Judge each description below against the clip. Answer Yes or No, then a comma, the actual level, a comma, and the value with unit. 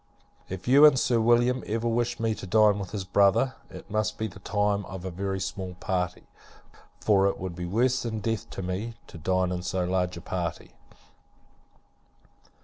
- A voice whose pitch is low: Yes, low, 100 Hz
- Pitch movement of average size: Yes, average, 3.6 semitones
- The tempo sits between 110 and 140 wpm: No, average, 185 wpm